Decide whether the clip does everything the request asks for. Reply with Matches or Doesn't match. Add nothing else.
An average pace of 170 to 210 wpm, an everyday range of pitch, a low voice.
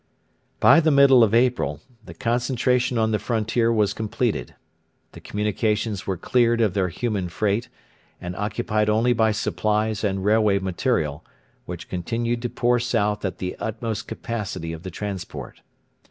Doesn't match